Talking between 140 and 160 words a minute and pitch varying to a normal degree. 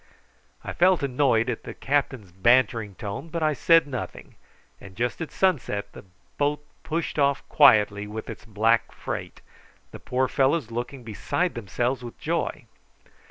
Yes: average, 150 wpm; average, 4.7 semitones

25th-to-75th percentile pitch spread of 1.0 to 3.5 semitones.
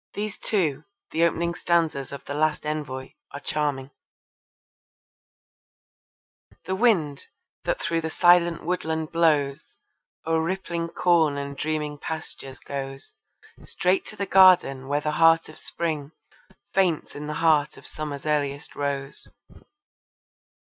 Yes: average, 3.0 semitones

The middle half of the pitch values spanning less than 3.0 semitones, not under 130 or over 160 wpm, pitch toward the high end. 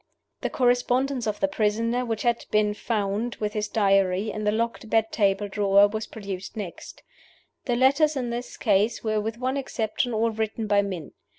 No: narrow, 2.5 semitones; average, 180 wpm; high, 220 Hz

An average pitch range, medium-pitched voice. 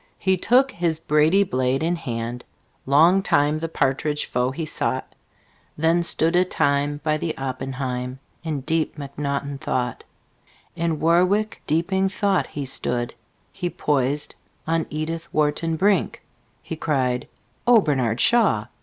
Yes: average, 4.1 semitones; medium, 155 Hz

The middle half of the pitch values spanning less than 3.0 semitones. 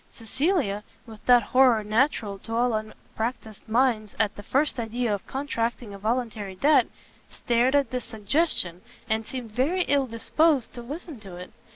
No: average, 3.5 semitones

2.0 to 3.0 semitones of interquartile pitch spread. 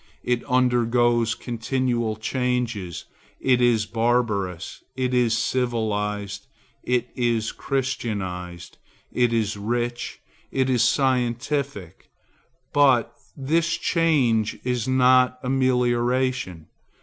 Yes: narrow, 2.5 semitones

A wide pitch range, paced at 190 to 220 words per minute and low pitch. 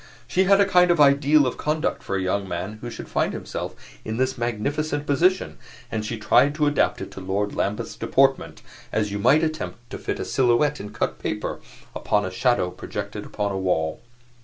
Yes: wide, 6.4 semitones; average, 200 wpm; low, 120 Hz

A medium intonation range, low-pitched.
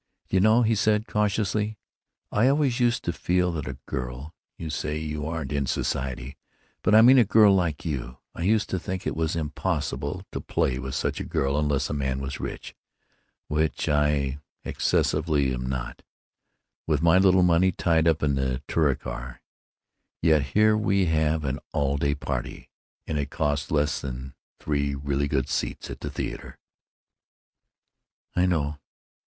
Yes: average, 5.0 semitones; very low, 75 Hz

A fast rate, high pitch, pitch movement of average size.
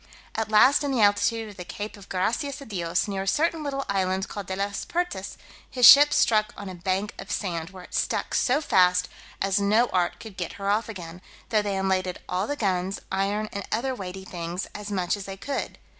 Yes: fast, 220 wpm; high, 200 Hz; average, 3.1 semitones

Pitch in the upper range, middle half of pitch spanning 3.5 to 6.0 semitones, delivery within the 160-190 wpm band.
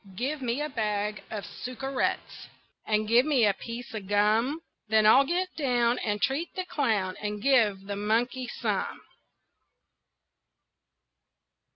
No: high, 235 Hz; average, 4.2 semitones; slow, 135 wpm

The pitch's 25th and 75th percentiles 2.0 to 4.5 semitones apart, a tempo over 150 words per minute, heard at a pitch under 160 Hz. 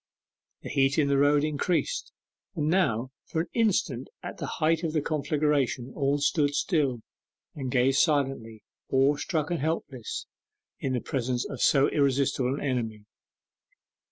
No: average, 2.9 semitones; average, 145 wpm; medium, 140 Hz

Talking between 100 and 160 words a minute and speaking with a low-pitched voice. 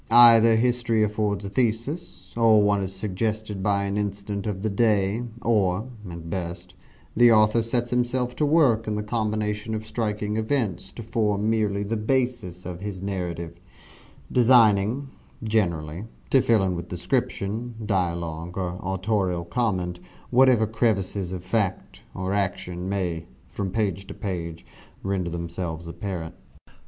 Yes: average, 140 wpm; low, 105 Hz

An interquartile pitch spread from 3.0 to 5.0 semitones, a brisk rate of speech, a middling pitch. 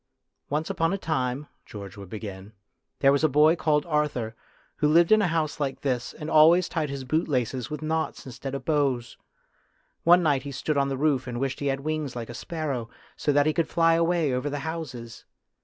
Yes: average, 3.6 semitones; fast, 210 wpm; medium, 145 Hz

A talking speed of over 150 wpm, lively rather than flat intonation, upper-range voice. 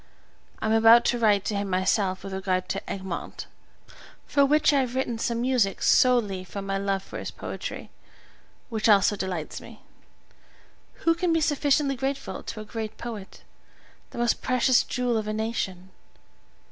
No: average, 165 wpm; average, 4.3 semitones; high, 220 Hz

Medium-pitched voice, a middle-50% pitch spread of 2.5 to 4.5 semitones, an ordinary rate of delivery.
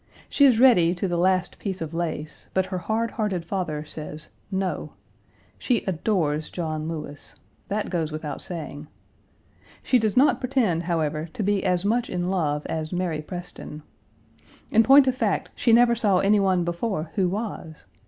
No: medium, 180 Hz; average, 4.9 semitones; average, 165 wpm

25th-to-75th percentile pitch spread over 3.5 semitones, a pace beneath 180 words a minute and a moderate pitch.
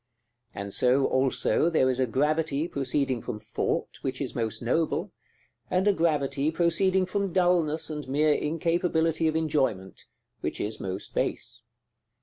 Yes: average, 4.4 semitones; average, 140 wpm; medium, 150 Hz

